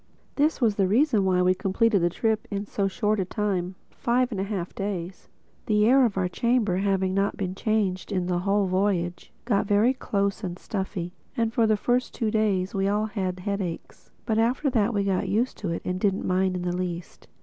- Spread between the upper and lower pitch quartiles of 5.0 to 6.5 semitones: No, average, 2.9 semitones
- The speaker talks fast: Yes, fast, 210 wpm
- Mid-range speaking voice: No, high, 200 Hz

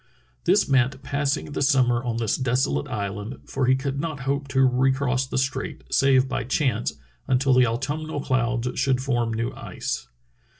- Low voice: Yes, low, 130 Hz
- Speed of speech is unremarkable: Yes, average, 165 wpm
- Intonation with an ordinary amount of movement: No, narrow, 2.1 semitones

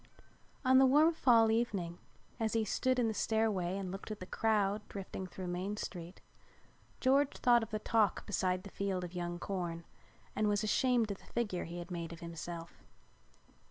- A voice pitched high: Yes, high, 200 Hz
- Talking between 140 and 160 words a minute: No, average, 185 wpm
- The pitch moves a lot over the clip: No, average, 4.0 semitones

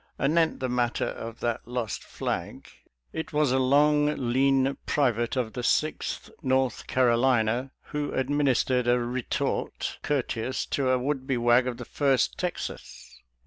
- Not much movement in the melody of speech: Yes, narrow, 2.3 semitones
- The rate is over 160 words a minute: No, average, 145 wpm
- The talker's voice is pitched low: Yes, low, 130 Hz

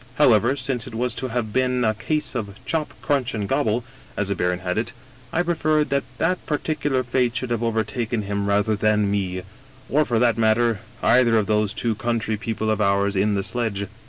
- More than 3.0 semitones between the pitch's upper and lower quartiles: Yes, average, 3.6 semitones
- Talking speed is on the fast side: Yes, fast, 215 wpm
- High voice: No, low, 115 Hz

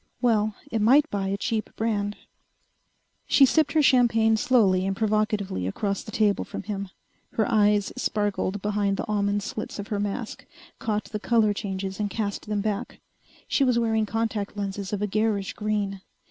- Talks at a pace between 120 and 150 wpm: No, average, 170 wpm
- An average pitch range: No, narrow, 1.8 semitones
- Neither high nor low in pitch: No, high, 210 Hz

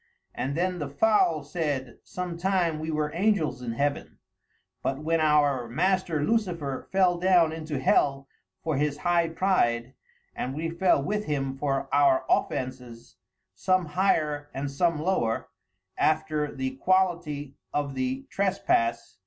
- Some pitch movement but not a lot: Yes, average, 4.4 semitones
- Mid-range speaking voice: Yes, medium, 150 Hz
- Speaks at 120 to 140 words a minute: Yes, slow, 135 wpm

